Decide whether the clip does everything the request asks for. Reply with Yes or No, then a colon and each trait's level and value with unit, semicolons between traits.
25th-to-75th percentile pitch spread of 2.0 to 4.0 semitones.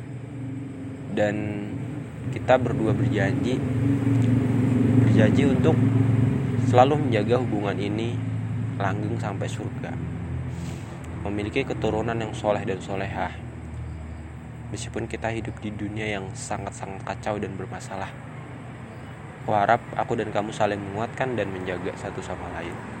Yes: average, 3.6 semitones